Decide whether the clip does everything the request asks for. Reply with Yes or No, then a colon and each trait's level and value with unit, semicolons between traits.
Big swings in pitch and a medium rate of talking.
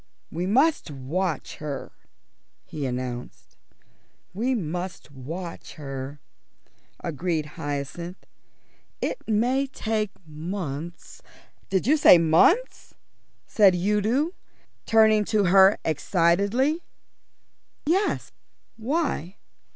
No: wide, 6.4 semitones; slow, 90 wpm